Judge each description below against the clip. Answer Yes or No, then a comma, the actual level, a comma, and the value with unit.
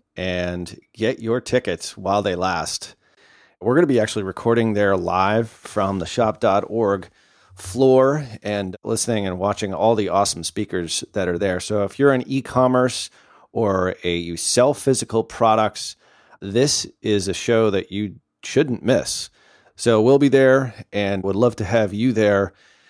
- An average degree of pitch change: Yes, average, 3.6 semitones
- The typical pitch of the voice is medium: No, low, 105 Hz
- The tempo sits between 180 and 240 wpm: No, average, 160 wpm